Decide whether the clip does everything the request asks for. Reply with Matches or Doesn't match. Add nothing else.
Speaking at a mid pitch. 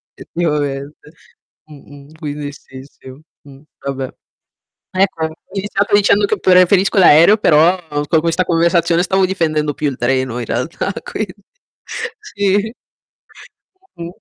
Matches